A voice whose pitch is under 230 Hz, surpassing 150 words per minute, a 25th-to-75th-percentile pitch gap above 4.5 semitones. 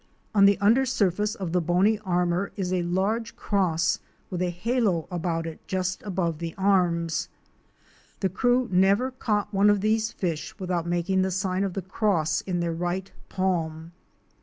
No: medium, 185 Hz; average, 165 wpm; average, 2.8 semitones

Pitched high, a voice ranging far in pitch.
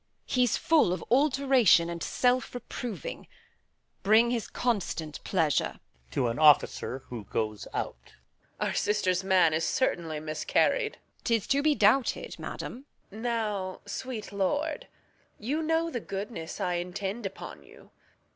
Yes: high, 210 Hz; wide, 6.6 semitones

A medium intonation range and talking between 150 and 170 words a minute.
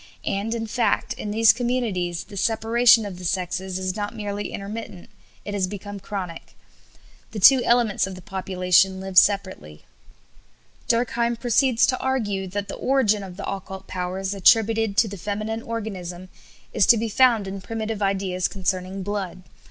Yes: average, 3.1 semitones; average, 160 wpm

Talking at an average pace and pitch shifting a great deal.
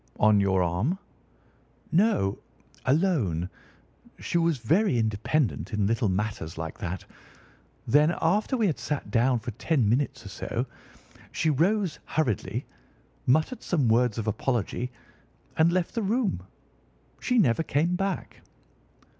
No: slow, 130 wpm; wide, 8.1 semitones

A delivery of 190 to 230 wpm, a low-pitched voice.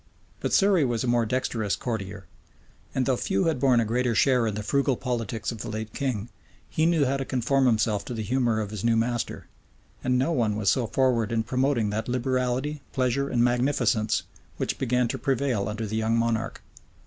Yes: average, 200 wpm; low, 120 Hz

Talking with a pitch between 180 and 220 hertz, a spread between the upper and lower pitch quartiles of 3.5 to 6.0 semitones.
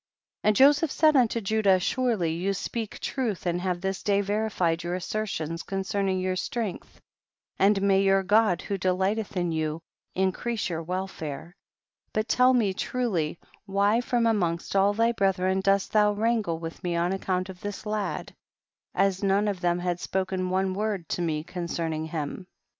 No: high, 190 Hz; average, 3.1 semitones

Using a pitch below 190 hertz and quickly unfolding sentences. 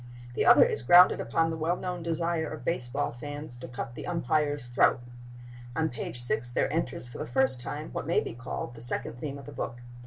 Yes: medium, 140 Hz; fast, 215 wpm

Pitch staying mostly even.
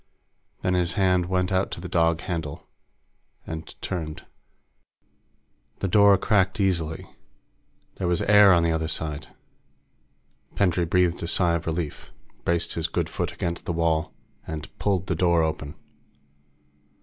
Yes: narrow, 2.3 semitones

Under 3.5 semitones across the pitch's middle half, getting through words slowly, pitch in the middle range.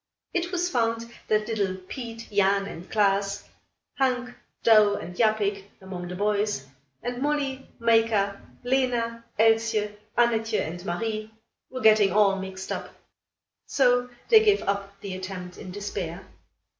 No: average, 3.1 semitones; slow, 130 wpm; high, 215 Hz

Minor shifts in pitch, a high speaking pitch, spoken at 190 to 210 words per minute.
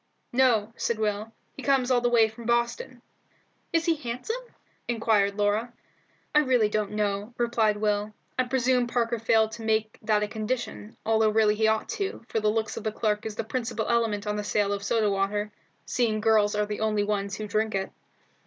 Yes: narrow, 2.1 semitones; high, 220 Hz; average, 195 wpm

